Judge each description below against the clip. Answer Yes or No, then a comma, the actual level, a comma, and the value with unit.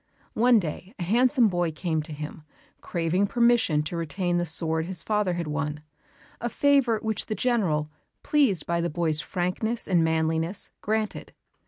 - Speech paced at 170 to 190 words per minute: No, average, 160 wpm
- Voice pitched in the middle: Yes, medium, 175 Hz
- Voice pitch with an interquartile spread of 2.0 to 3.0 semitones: No, average, 5.3 semitones